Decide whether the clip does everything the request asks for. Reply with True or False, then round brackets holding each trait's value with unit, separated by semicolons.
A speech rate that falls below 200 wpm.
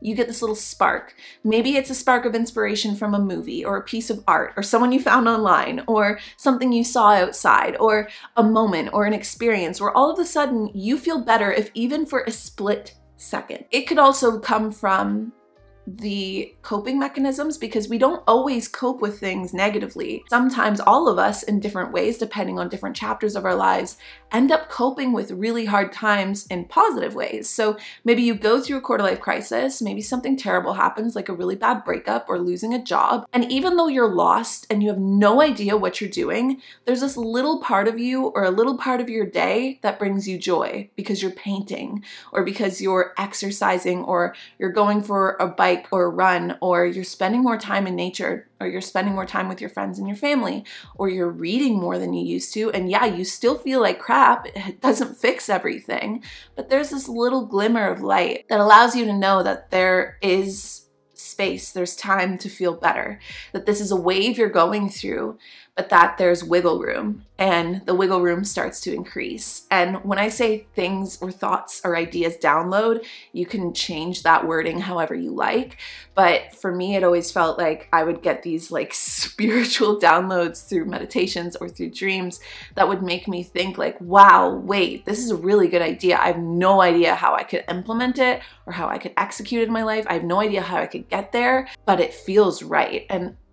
False (205 wpm)